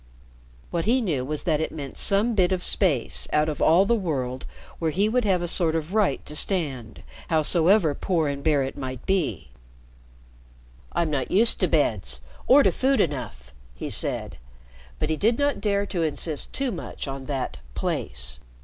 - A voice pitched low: No, medium, 160 Hz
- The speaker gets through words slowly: No, average, 180 wpm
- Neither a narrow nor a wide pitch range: No, wide, 6.1 semitones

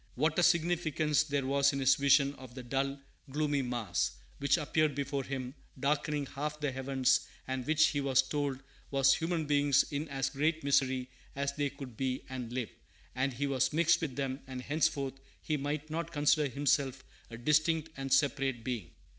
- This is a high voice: No, medium, 140 Hz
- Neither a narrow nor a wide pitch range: No, narrow, 2.2 semitones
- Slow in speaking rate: No, average, 180 wpm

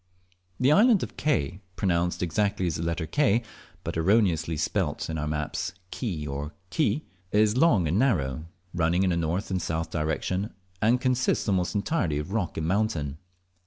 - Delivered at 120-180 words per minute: Yes, average, 165 wpm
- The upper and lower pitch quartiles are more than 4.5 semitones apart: Yes, average, 5.3 semitones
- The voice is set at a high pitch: No, very low, 90 Hz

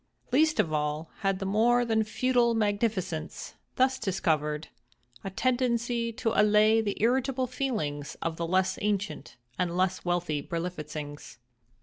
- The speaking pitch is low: No, high, 205 Hz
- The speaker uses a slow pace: Yes, slow, 130 wpm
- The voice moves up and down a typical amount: No, wide, 5.9 semitones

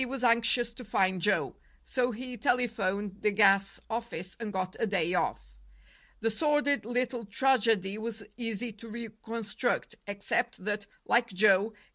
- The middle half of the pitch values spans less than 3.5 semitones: Yes, average, 3.1 semitones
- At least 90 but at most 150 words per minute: Yes, average, 145 wpm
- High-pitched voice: Yes, high, 220 Hz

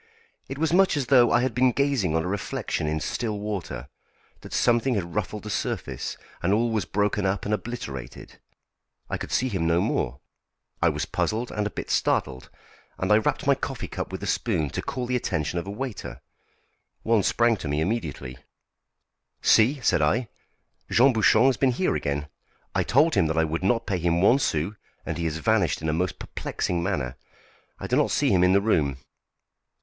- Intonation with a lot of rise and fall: Yes, wide, 6.6 semitones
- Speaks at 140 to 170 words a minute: No, average, 200 wpm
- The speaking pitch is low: Yes, low, 100 Hz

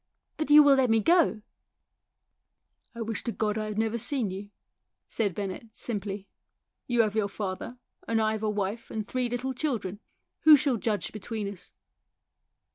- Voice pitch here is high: Yes, high, 220 Hz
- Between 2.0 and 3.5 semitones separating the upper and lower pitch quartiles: Yes, average, 3.0 semitones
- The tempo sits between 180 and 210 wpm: Yes, average, 190 wpm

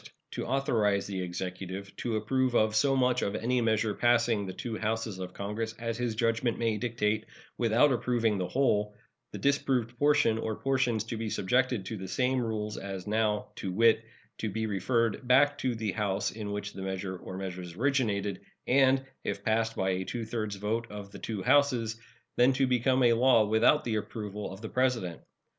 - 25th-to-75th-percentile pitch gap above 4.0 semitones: No, average, 3.2 semitones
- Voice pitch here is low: Yes, low, 110 Hz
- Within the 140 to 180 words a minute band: No, average, 190 wpm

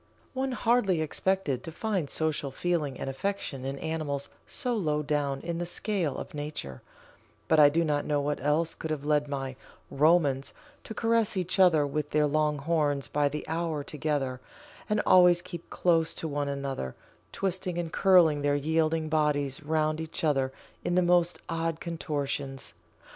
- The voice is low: No, medium, 155 Hz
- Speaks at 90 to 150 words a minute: No, average, 165 wpm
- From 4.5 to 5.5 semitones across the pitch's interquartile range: No, average, 3.2 semitones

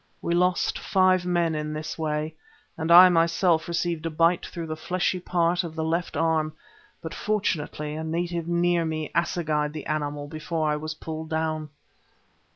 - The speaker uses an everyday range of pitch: No, narrow, 1.8 semitones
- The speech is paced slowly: No, average, 165 wpm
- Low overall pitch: No, medium, 160 Hz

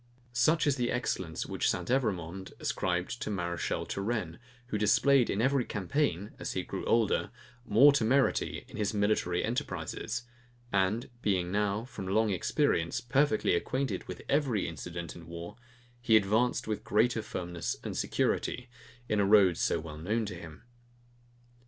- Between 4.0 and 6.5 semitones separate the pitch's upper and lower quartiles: Yes, average, 5.2 semitones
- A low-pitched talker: Yes, low, 105 Hz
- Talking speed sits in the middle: Yes, average, 145 wpm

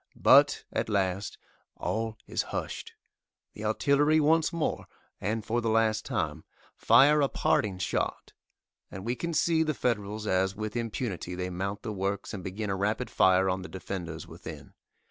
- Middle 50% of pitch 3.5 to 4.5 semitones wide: Yes, average, 4.1 semitones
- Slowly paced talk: No, average, 165 wpm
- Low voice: Yes, low, 105 Hz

